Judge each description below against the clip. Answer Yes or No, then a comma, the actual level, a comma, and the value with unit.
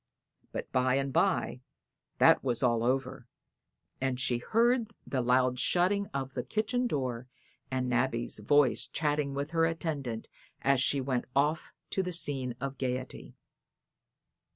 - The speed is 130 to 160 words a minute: Yes, average, 140 wpm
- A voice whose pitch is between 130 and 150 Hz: Yes, low, 135 Hz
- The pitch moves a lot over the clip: No, average, 3.8 semitones